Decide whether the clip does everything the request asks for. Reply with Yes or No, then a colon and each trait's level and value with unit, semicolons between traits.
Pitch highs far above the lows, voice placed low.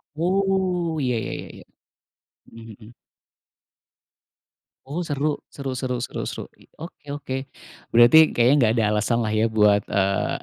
Yes: wide, 5.9 semitones; low, 130 Hz